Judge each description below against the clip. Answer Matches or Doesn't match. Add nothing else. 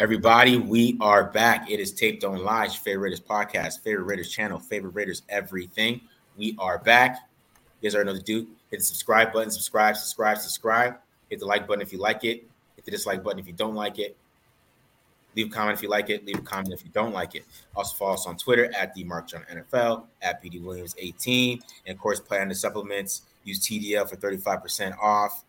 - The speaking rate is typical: Doesn't match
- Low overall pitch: Matches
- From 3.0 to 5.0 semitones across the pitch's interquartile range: Doesn't match